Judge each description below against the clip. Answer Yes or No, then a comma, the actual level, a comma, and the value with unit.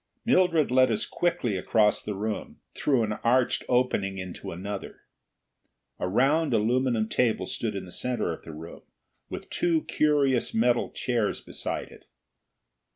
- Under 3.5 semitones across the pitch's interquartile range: No, average, 4.1 semitones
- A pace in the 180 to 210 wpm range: No, average, 145 wpm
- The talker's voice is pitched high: No, low, 120 Hz